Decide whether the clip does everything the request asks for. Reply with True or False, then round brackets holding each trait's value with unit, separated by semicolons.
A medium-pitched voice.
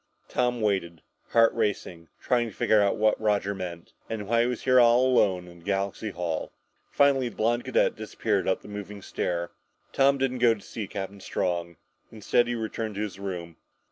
False (105 Hz)